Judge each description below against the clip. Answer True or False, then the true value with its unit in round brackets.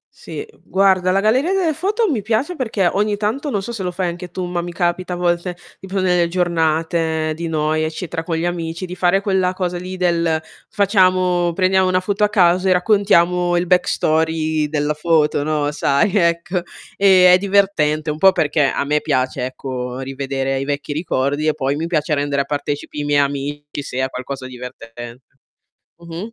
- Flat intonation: False (3.9 semitones)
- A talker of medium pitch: True (170 Hz)